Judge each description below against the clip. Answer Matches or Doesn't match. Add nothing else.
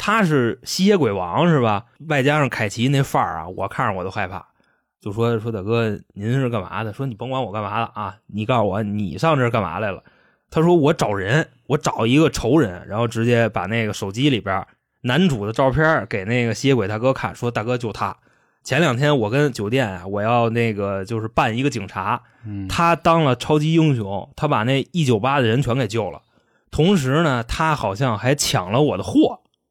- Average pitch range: Matches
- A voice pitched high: Doesn't match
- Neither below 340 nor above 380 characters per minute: Doesn't match